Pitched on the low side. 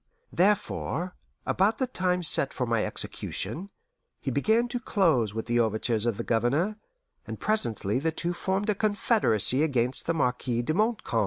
No: medium, 160 Hz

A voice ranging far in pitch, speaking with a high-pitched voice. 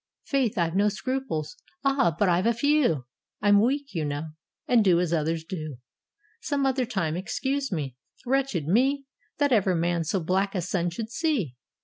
Yes: wide, 8.0 semitones; high, 200 Hz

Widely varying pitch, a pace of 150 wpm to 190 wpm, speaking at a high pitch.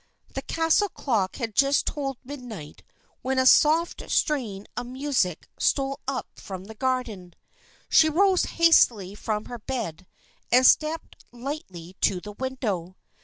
No: wide, 6.2 semitones; slow, 135 wpm; very high, 250 Hz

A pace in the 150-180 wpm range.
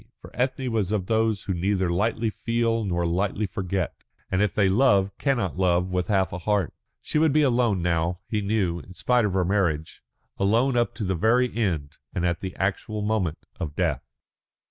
No: average, 190 wpm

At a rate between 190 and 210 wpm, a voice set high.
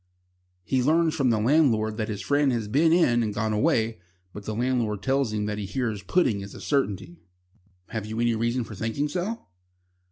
No: average, 195 wpm; low, 115 Hz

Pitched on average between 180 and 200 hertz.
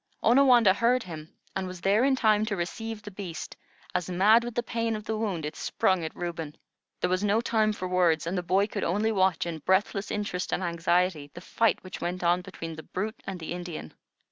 Yes: medium, 185 Hz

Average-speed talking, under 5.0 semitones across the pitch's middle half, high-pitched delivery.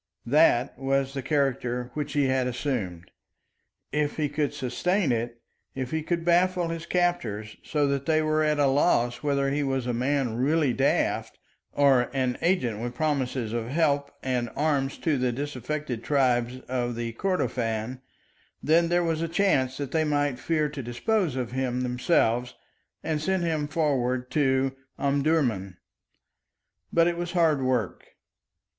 No: average, 150 wpm; average, 3.8 semitones; low, 135 Hz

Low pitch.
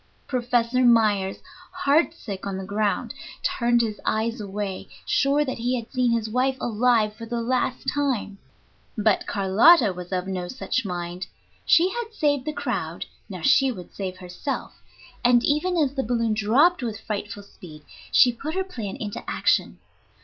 No: high, 230 Hz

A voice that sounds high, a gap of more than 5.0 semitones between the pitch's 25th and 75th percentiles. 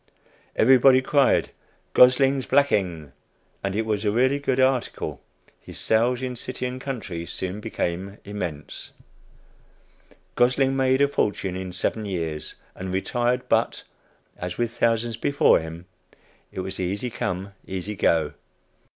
No: low, 110 Hz; wide, 5.5 semitones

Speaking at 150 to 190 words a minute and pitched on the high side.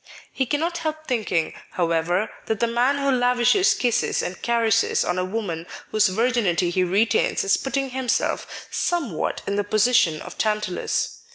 Yes: average, 155 wpm; high, 225 Hz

